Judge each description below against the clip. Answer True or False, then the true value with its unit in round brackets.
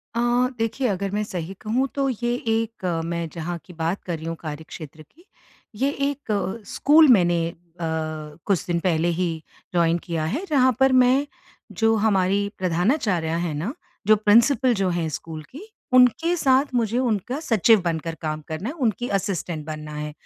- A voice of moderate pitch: False (195 Hz)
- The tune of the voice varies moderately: False (6.6 semitones)